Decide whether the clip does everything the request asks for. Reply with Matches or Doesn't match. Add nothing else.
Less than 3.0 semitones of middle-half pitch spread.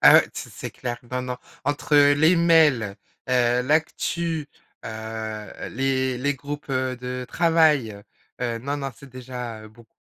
Doesn't match